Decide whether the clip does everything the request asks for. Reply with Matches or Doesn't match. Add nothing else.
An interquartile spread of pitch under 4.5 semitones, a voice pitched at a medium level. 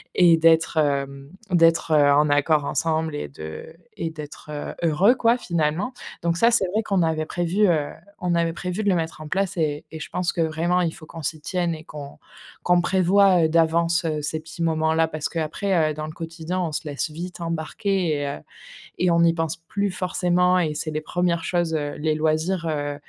Matches